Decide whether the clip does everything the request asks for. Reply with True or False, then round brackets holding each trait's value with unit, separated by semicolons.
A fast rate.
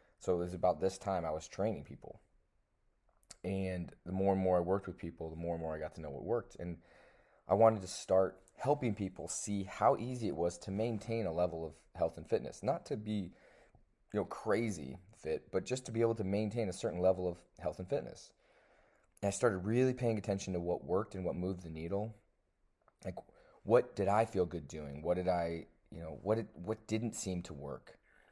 True (220 wpm)